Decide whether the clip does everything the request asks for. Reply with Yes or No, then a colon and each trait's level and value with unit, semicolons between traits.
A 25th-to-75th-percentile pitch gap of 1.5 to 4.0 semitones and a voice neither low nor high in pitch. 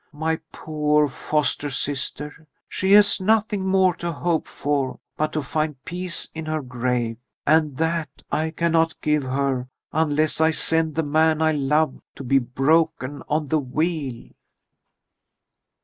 Yes: narrow, 2.5 semitones; medium, 155 Hz